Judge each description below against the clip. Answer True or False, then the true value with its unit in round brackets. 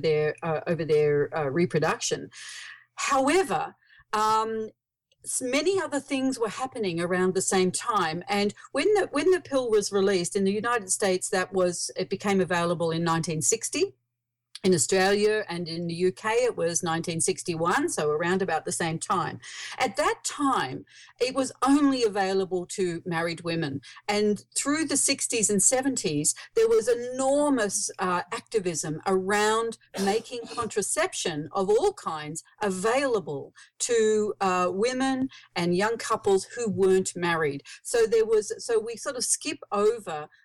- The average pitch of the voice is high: True (205 Hz)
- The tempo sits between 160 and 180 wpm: False (145 wpm)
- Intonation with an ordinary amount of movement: False (7.1 semitones)